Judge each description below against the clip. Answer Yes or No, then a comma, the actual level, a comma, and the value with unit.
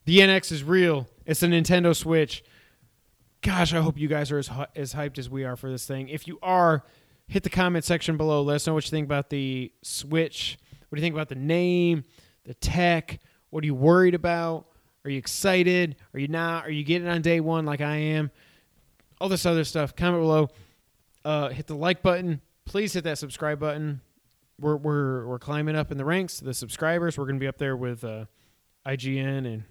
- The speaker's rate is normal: No, fast, 215 wpm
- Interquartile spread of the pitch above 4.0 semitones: No, average, 3.6 semitones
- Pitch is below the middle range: No, medium, 150 Hz